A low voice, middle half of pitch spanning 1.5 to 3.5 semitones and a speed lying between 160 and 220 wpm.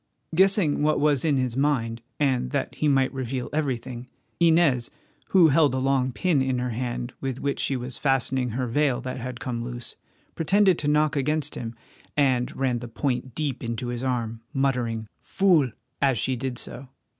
Yes: low, 130 Hz; average, 3.1 semitones; average, 180 wpm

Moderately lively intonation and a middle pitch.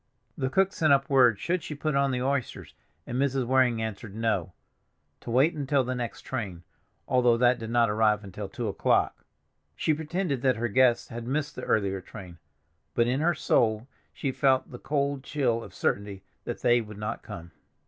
No: average, 3.8 semitones; low, 125 Hz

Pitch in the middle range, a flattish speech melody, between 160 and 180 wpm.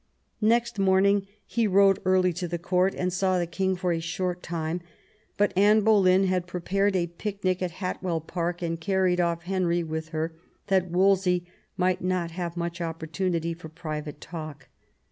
Yes: medium, 180 Hz; narrow, 2.1 semitones; average, 165 wpm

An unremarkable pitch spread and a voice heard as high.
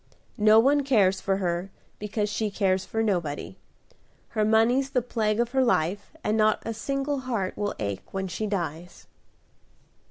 Yes: average, 3.9 semitones; high, 210 Hz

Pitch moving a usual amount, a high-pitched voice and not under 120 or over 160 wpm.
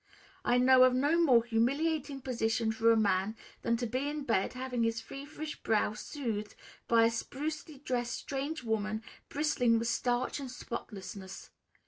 Yes: average, 3.5 semitones; high, 245 Hz; average, 155 wpm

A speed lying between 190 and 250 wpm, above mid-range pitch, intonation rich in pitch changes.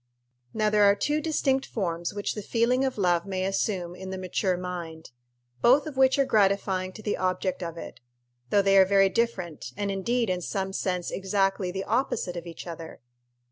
No: average, 195 wpm; high, 195 Hz; average, 3.0 semitones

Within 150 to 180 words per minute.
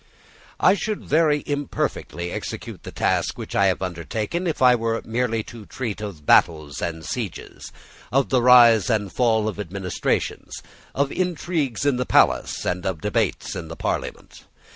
Yes: average, 160 wpm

